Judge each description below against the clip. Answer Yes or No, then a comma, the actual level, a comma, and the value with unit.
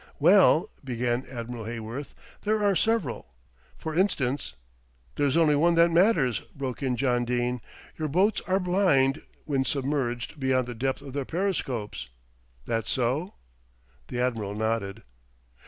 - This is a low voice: Yes, low, 130 Hz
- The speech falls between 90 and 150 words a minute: Yes, average, 140 wpm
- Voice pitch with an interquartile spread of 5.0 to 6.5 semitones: Yes, wide, 5.4 semitones